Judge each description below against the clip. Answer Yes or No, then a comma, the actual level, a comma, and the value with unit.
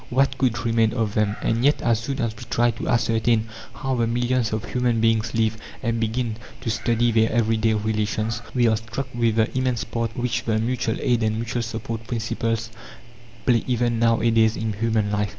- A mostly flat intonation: Yes, narrow, 1.4 semitones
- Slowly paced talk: No, average, 200 wpm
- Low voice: Yes, low, 115 Hz